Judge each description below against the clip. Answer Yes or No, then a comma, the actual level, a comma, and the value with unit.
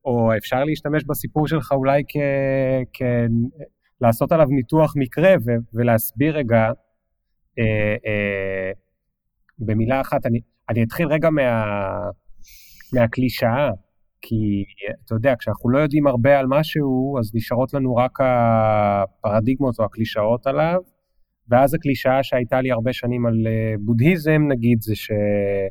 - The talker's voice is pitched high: No, low, 120 Hz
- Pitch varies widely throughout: No, average, 4.0 semitones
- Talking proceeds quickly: No, average, 120 wpm